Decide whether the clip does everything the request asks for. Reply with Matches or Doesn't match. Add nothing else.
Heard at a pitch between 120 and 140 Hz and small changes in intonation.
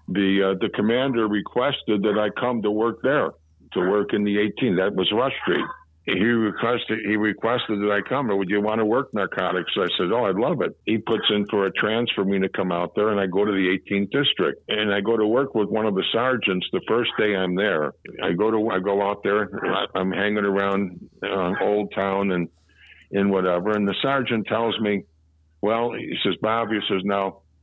Doesn't match